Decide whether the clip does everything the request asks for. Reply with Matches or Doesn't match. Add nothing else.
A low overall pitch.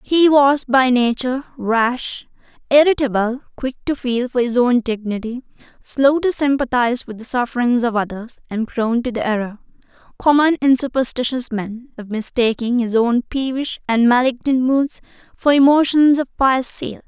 Doesn't match